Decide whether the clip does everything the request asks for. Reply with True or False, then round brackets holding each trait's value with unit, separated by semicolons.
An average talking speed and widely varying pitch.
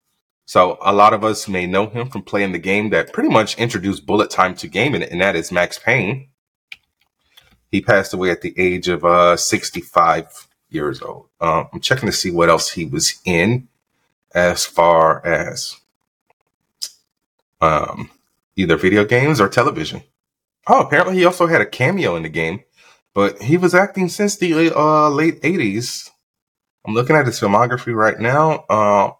True (170 wpm; 8.3 semitones)